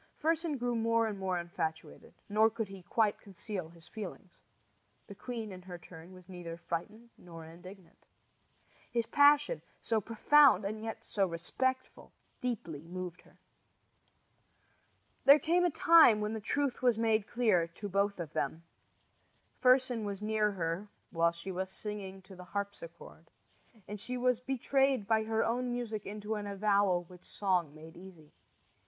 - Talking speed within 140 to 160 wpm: Yes, average, 155 wpm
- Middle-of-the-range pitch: No, high, 205 Hz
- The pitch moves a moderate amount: Yes, average, 4.4 semitones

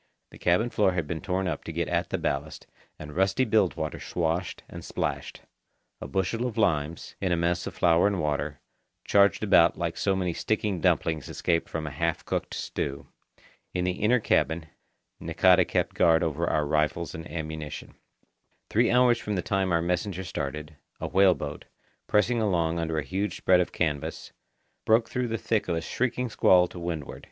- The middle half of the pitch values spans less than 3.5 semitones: No, average, 3.9 semitones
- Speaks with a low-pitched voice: Yes, very low, 90 Hz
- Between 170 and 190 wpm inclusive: Yes, average, 185 wpm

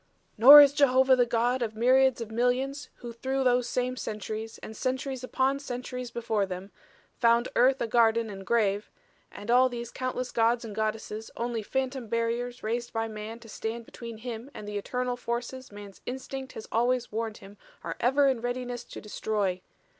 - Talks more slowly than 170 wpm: No, average, 175 wpm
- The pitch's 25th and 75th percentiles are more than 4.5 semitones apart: No, narrow, 2.4 semitones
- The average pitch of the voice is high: Yes, high, 235 Hz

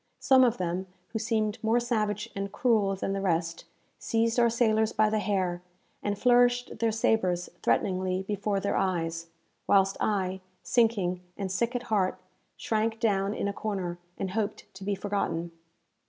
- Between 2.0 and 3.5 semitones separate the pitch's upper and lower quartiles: Yes, average, 3.0 semitones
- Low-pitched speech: No, high, 205 Hz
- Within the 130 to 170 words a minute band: Yes, average, 160 wpm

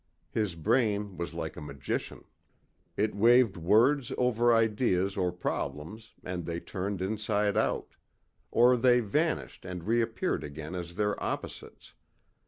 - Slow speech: Yes, slow, 130 wpm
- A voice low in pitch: Yes, low, 105 Hz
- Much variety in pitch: No, average, 4.6 semitones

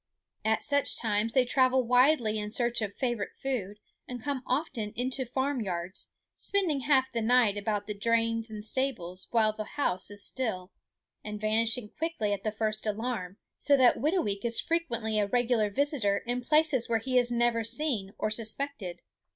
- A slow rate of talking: No, average, 175 wpm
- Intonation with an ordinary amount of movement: Yes, average, 3.7 semitones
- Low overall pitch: No, high, 230 Hz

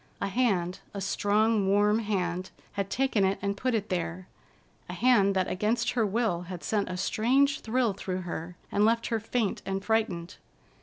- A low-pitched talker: No, high, 200 Hz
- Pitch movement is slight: No, average, 3.3 semitones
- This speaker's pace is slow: No, average, 175 wpm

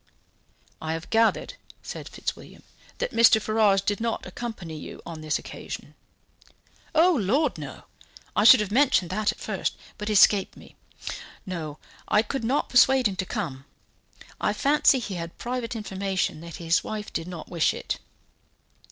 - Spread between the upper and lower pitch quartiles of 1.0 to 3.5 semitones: No, average, 5.3 semitones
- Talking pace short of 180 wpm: Yes, average, 160 wpm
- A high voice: Yes, high, 210 Hz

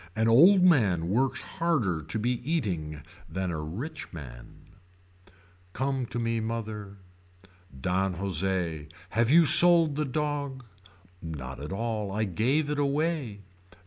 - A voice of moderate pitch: No, low, 110 Hz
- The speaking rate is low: Yes, slow, 130 wpm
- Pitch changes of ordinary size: No, wide, 7.7 semitones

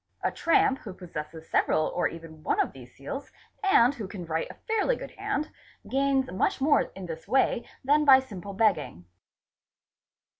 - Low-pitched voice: No, high, 210 Hz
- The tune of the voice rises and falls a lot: Yes, wide, 9.0 semitones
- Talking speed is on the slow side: No, average, 180 wpm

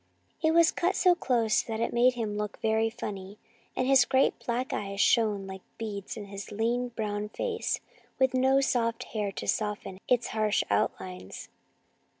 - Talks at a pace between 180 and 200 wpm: No, average, 165 wpm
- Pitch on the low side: No, high, 225 Hz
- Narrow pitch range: No, average, 3.4 semitones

